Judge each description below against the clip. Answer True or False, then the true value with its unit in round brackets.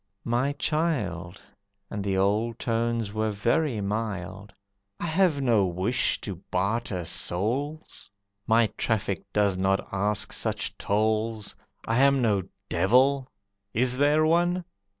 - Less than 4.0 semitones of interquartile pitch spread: False (5.1 semitones)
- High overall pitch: False (110 Hz)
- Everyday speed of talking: False (120 wpm)